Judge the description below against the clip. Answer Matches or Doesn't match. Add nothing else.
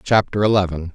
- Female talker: Doesn't match